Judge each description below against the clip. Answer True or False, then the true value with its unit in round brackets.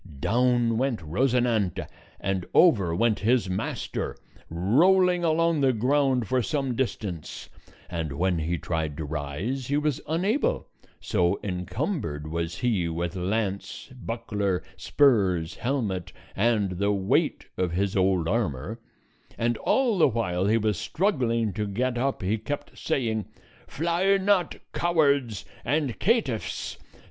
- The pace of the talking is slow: True (130 wpm)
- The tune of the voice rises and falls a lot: True (6.9 semitones)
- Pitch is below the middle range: True (115 Hz)